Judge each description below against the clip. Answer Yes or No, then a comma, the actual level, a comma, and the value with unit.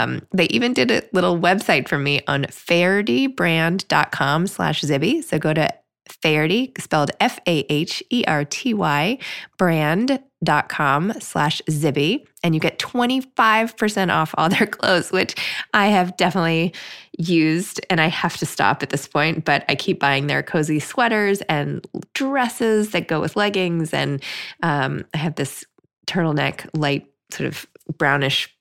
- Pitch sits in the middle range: Yes, medium, 165 Hz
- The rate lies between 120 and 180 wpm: Yes, average, 140 wpm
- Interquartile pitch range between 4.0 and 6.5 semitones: Yes, wide, 5.4 semitones